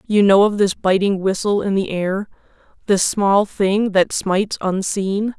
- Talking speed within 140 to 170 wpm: Yes, average, 155 wpm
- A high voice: Yes, high, 195 Hz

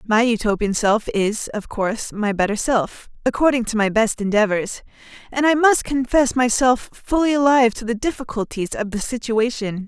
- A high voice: Yes, high, 230 Hz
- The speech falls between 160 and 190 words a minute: No, average, 150 wpm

